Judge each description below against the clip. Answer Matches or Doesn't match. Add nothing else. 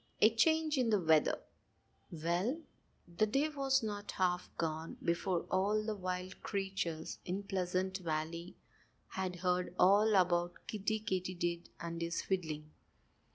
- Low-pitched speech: Doesn't match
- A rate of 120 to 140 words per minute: Matches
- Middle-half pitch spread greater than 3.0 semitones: Matches